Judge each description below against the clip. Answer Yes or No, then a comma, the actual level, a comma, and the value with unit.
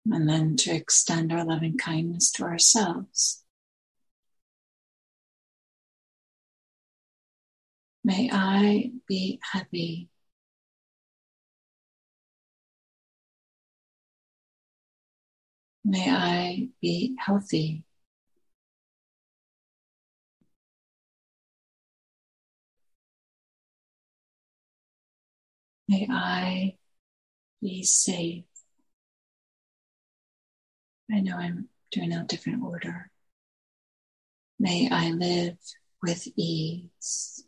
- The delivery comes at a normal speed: No, slow, 55 wpm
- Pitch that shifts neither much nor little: Yes, average, 3.8 semitones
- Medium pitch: Yes, medium, 180 Hz